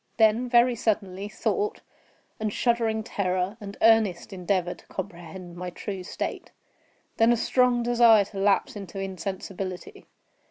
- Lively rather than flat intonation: No, average, 3.5 semitones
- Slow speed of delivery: Yes, slow, 130 wpm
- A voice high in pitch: Yes, high, 205 Hz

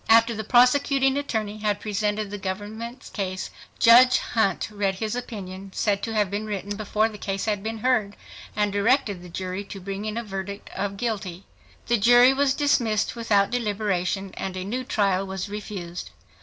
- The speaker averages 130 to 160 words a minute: No, average, 175 wpm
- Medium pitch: No, high, 210 Hz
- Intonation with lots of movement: No, average, 2.8 semitones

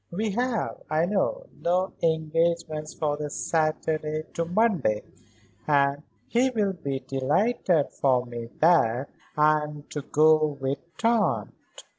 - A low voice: No, medium, 155 Hz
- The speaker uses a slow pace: Yes, slow, 125 wpm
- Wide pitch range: No, average, 4.1 semitones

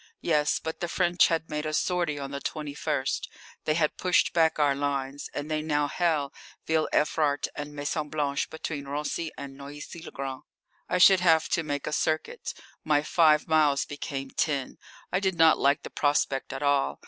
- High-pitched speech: No, medium, 150 Hz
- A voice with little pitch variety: Yes, narrow, 2.2 semitones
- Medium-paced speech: Yes, average, 185 wpm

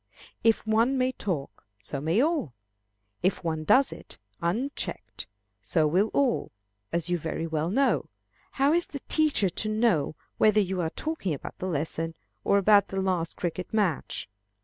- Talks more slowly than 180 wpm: Yes, average, 160 wpm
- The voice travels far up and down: Yes, wide, 6.2 semitones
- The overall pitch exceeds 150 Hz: Yes, high, 190 Hz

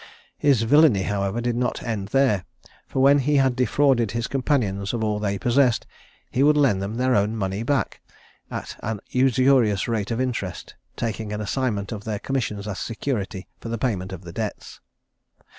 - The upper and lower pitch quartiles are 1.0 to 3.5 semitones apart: No, average, 4.3 semitones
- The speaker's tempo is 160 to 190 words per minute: Yes, average, 175 wpm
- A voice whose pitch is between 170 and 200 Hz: No, low, 115 Hz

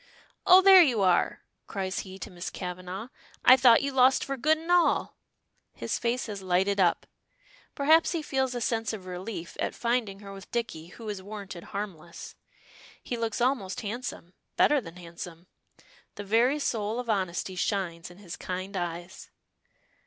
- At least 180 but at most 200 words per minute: No, average, 165 wpm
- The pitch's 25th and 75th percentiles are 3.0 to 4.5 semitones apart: No, average, 5.3 semitones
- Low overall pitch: No, high, 205 Hz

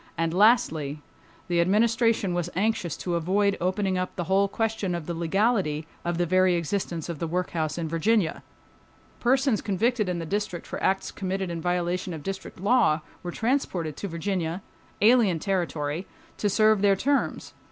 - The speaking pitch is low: No, medium, 185 Hz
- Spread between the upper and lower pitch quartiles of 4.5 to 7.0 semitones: No, average, 3.4 semitones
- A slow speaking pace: No, average, 155 wpm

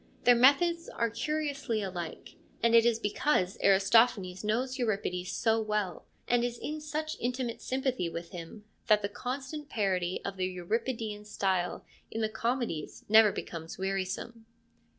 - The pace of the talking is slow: No, average, 145 wpm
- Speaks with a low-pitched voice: No, high, 220 Hz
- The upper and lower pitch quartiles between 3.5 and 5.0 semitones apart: Yes, average, 4.5 semitones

